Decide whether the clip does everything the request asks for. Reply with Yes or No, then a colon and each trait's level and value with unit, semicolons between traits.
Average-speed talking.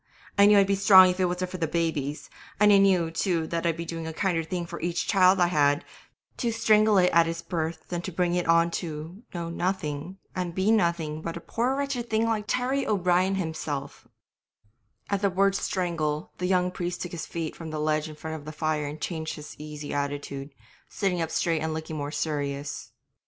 No: fast, 215 wpm